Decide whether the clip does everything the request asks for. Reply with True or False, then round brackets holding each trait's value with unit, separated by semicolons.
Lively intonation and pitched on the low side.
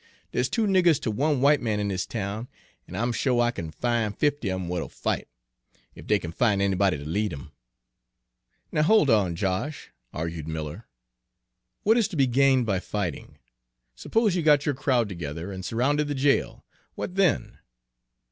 True (7.5 semitones; 115 Hz)